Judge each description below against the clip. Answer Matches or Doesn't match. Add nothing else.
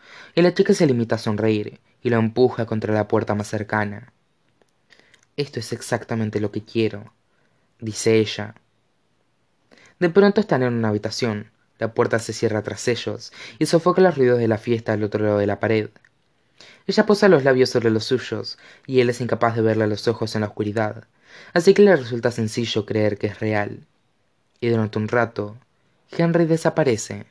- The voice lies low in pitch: Matches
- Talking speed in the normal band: Matches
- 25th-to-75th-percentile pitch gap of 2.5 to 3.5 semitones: Matches